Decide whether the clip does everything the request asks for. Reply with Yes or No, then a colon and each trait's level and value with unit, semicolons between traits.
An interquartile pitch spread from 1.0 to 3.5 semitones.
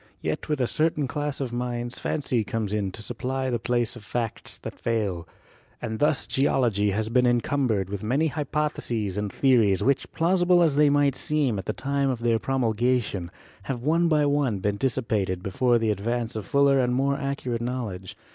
No: average, 4.2 semitones